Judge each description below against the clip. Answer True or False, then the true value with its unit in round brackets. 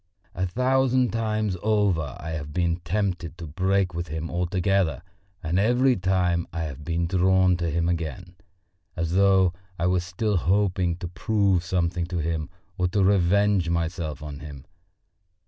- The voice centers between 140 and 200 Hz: False (90 Hz)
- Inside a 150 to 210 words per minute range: True (155 wpm)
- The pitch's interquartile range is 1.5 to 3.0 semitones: True (2.7 semitones)